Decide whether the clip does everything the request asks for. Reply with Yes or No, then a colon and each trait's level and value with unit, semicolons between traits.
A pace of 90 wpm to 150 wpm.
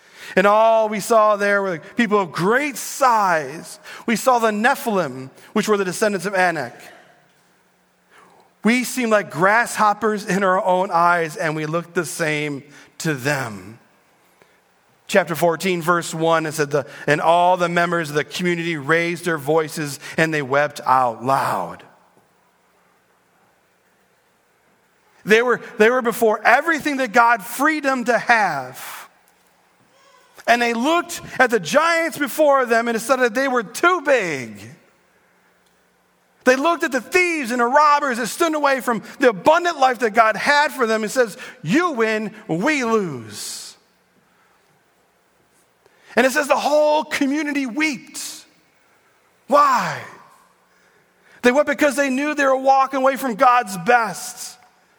Yes: average, 140 wpm